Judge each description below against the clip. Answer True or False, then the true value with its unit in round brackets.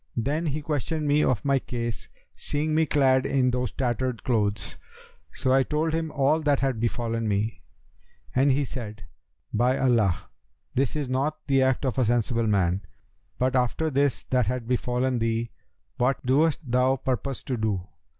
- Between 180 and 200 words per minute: False (165 wpm)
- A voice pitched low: True (130 Hz)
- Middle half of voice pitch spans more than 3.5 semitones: False (3.1 semitones)